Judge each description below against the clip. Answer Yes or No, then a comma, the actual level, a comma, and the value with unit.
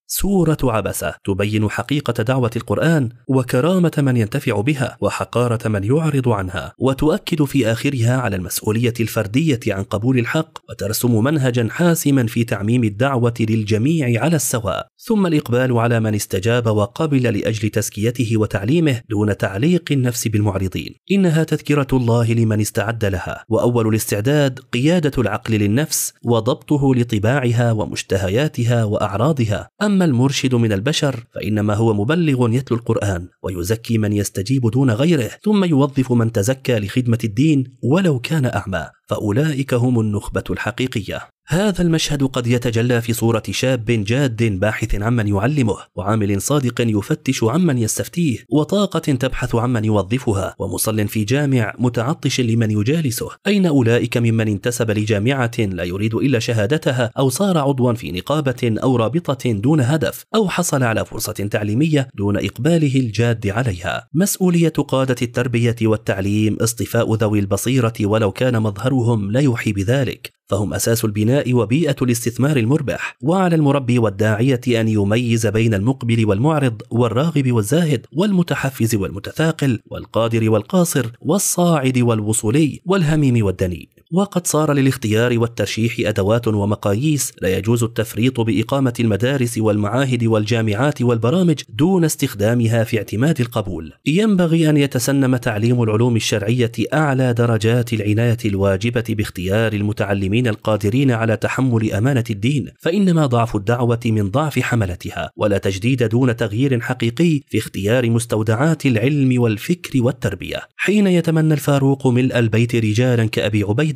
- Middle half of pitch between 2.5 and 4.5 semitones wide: Yes, average, 4.1 semitones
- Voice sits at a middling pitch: No, low, 120 Hz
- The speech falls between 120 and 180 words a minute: Yes, average, 125 wpm